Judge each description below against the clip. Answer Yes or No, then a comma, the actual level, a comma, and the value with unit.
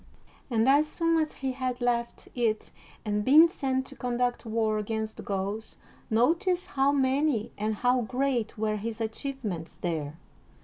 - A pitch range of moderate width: Yes, average, 3.9 semitones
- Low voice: No, high, 245 Hz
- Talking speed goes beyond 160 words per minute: No, average, 150 wpm